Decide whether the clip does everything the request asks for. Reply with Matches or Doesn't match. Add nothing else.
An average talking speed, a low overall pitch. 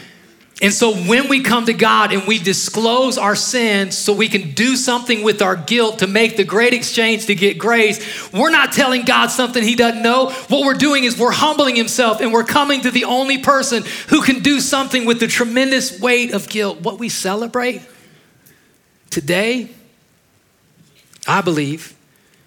Doesn't match